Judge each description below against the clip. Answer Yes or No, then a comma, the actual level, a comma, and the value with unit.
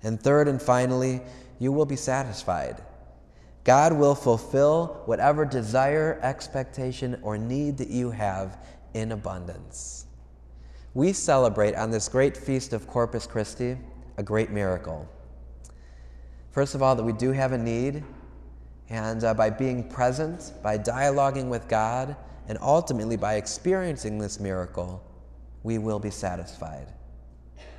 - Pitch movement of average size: No, wide, 7.1 semitones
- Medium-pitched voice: No, low, 110 Hz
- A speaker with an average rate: No, slow, 130 wpm